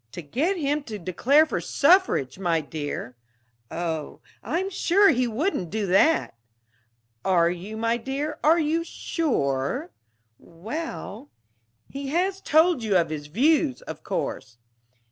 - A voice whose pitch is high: Yes, high, 235 Hz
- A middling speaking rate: No, slow, 130 wpm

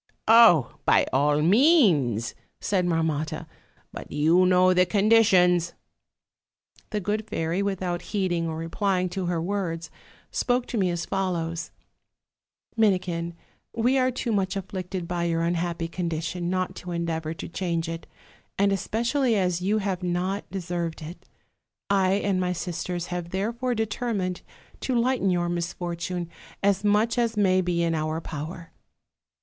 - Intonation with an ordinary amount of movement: Yes, average, 3.1 semitones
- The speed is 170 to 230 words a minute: No, average, 140 wpm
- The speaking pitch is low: No, medium, 180 Hz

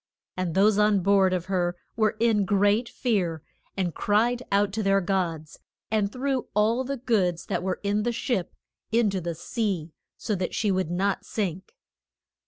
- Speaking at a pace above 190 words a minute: No, average, 175 wpm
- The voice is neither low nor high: No, high, 200 Hz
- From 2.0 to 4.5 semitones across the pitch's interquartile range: Yes, average, 3.0 semitones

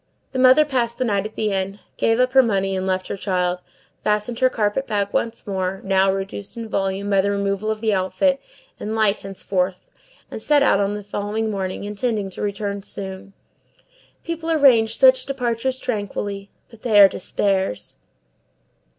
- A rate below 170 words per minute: No, average, 175 wpm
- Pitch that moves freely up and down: No, average, 3.2 semitones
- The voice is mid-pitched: No, high, 205 Hz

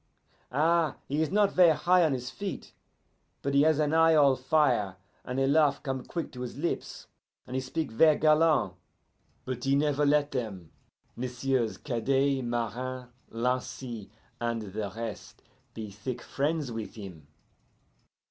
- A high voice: No, low, 135 Hz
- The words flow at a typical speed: Yes, average, 150 wpm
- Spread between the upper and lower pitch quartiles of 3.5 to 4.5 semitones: Yes, average, 4.2 semitones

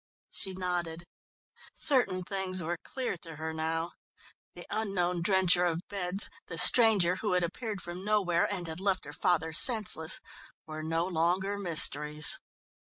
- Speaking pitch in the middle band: Yes, medium, 180 Hz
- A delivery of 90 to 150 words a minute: Yes, average, 145 wpm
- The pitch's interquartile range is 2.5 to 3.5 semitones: Yes, average, 3.1 semitones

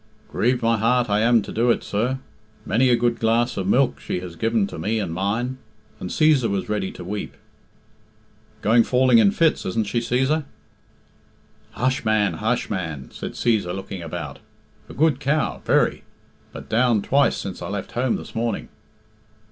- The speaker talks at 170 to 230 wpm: Yes, average, 175 wpm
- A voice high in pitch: No, low, 115 Hz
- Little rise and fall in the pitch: No, average, 3.7 semitones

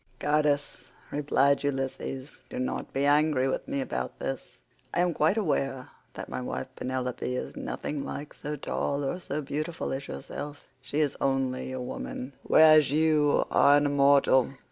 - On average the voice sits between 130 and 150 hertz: Yes, medium, 140 Hz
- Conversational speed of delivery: Yes, average, 160 wpm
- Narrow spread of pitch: Yes, narrow, 2.1 semitones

